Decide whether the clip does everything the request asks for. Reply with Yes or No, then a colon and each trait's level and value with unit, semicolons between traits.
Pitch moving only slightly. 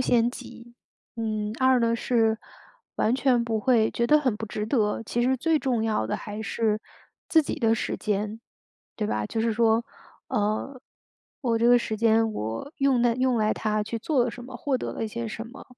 Yes: narrow, 2.3 semitones